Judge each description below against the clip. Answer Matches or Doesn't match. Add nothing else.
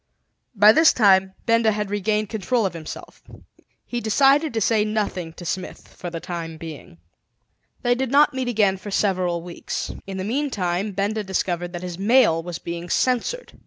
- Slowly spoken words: Doesn't match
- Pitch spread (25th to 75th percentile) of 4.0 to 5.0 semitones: Matches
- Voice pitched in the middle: Doesn't match